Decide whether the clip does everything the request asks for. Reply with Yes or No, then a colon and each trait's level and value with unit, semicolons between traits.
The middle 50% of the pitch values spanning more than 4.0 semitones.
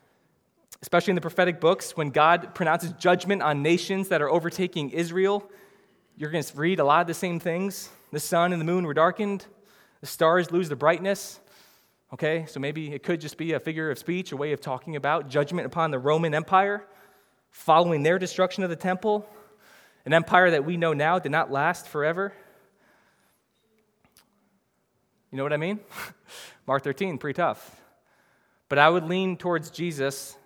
No: average, 3.6 semitones